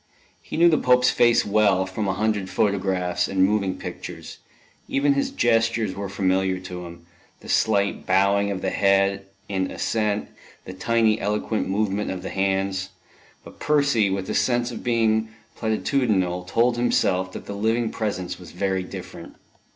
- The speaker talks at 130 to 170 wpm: Yes, average, 160 wpm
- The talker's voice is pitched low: Yes, low, 100 Hz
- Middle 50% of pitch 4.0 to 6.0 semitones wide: No, average, 3.0 semitones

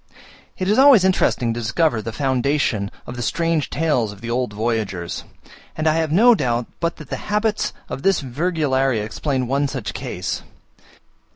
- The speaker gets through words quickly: No, average, 170 wpm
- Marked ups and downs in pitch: Yes, wide, 5.9 semitones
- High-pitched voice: No, low, 135 Hz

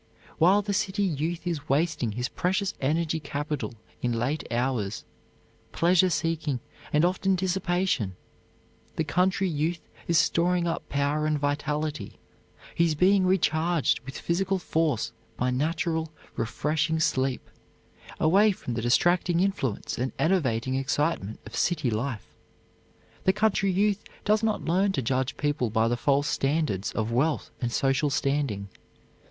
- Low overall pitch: No, medium, 155 Hz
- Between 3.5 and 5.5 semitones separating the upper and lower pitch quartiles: Yes, average, 5.1 semitones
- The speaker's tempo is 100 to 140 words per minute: Yes, slow, 135 wpm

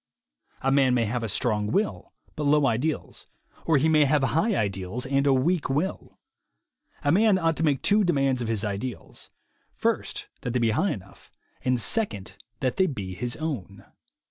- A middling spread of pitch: No, wide, 5.7 semitones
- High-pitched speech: No, low, 135 Hz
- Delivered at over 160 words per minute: Yes, average, 180 wpm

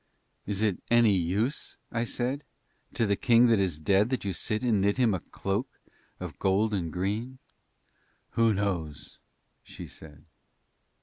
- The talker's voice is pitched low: Yes, low, 100 Hz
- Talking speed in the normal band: Yes, average, 150 wpm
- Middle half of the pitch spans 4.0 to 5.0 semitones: No, average, 3.5 semitones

